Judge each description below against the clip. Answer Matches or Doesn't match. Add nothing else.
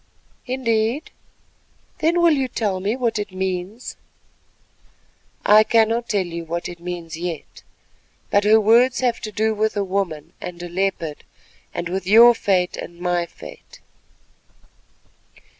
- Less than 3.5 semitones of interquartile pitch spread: Doesn't match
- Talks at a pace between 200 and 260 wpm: Doesn't match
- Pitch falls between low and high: Doesn't match